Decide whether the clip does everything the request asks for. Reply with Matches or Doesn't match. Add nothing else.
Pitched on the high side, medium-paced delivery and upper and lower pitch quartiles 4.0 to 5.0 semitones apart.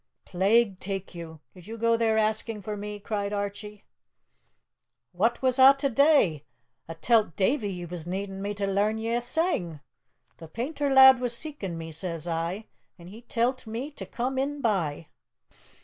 Matches